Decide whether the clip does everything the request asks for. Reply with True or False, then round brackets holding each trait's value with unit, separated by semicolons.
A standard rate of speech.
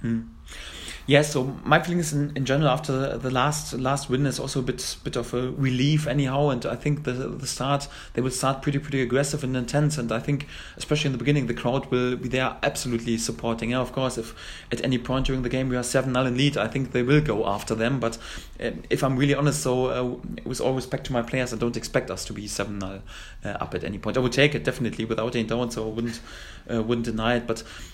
False (250 wpm)